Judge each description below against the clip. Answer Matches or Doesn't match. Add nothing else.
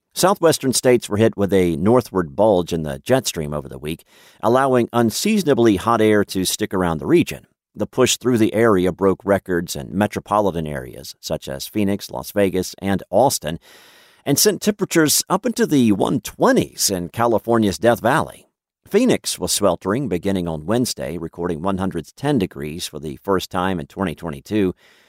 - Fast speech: Doesn't match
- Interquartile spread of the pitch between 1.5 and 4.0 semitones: Doesn't match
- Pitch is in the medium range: Doesn't match